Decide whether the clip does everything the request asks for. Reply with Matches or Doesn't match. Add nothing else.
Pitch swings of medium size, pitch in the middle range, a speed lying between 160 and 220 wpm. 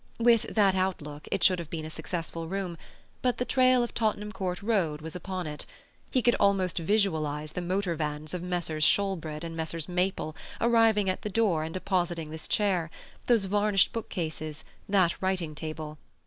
Matches